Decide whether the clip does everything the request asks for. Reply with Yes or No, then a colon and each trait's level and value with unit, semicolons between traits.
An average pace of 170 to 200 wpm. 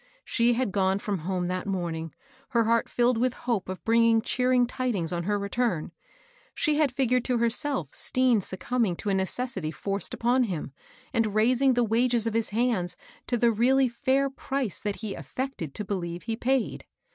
Yes: average, 180 wpm